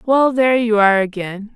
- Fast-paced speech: No, average, 195 wpm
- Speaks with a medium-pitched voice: No, high, 225 Hz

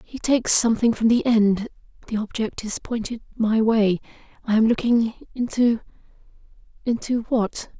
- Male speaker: No, female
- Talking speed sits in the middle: No, slow, 110 wpm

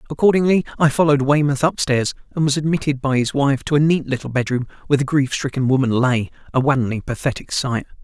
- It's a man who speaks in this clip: Yes, male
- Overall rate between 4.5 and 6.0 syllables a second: No, 6.2 syllables/s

